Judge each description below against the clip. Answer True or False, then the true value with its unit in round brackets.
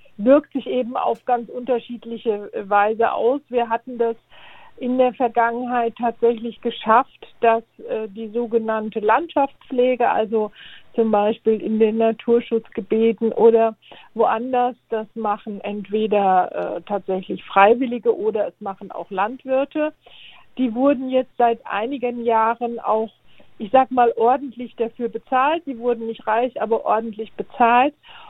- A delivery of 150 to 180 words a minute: False (125 wpm)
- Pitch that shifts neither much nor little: False (2.2 semitones)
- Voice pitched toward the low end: False (235 Hz)